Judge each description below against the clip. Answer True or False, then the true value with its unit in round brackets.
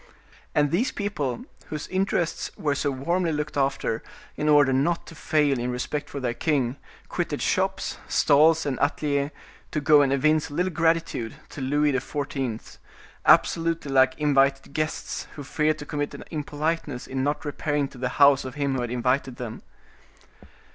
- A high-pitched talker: False (145 Hz)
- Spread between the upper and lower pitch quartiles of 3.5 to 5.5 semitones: False (2.5 semitones)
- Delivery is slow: False (165 wpm)